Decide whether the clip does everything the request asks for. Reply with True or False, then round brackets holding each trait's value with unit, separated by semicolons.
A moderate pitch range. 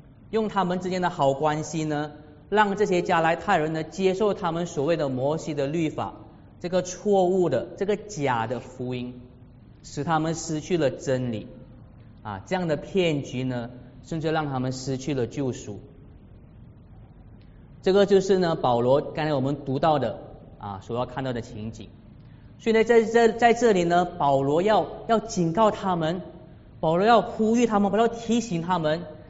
False (6.4 semitones)